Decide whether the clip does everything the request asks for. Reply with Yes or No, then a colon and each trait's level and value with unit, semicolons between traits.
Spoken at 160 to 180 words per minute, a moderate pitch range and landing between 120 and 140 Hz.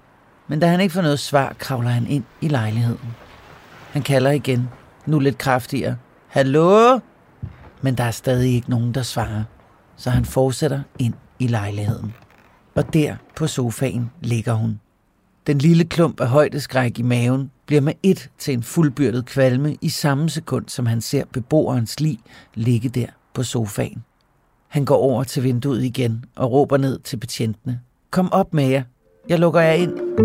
Yes: average, 165 wpm; average, 3.5 semitones; low, 130 Hz